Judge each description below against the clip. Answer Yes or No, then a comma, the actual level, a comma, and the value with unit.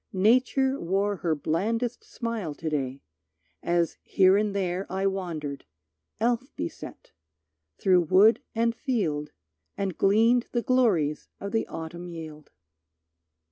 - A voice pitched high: Yes, high, 195 Hz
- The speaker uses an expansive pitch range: Yes, wide, 5.9 semitones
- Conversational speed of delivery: No, slow, 120 wpm